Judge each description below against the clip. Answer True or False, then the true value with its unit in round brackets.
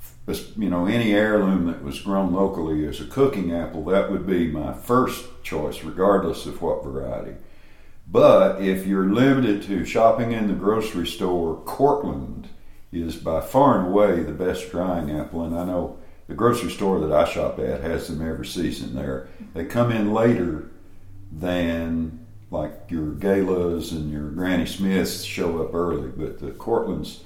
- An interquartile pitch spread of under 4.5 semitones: True (3.4 semitones)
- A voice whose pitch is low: True (90 Hz)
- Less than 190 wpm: True (165 wpm)